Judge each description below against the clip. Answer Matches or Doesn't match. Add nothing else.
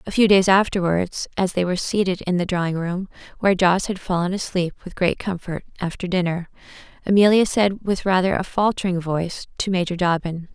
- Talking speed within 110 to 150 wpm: Doesn't match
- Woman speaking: Matches